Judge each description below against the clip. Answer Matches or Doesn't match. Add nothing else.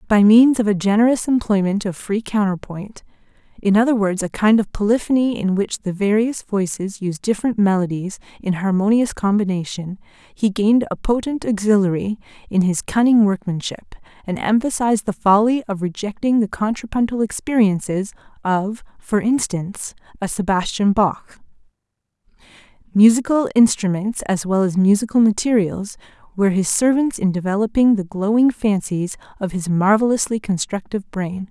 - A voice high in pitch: Matches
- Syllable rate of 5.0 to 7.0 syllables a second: Matches